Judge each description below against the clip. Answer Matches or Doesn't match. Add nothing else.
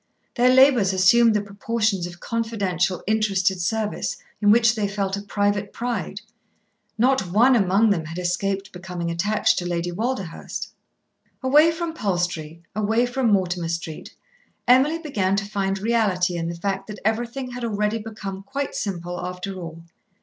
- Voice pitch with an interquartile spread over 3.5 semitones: Matches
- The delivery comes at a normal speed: Matches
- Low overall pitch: Doesn't match